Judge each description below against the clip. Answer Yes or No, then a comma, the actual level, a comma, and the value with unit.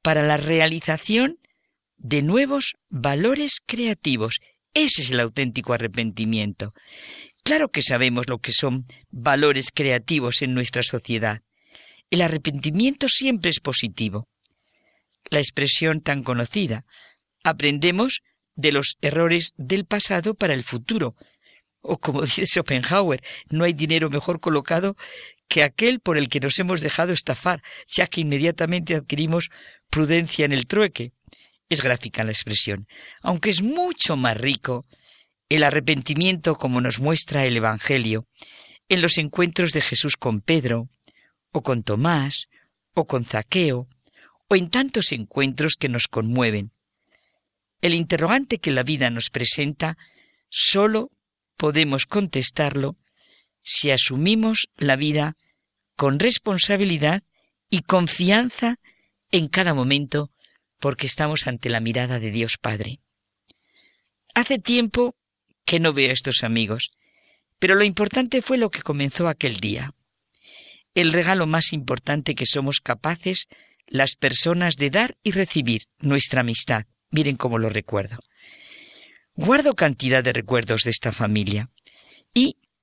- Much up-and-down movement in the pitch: Yes, wide, 5.9 semitones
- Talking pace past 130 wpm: No, slow, 125 wpm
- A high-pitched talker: No, medium, 150 Hz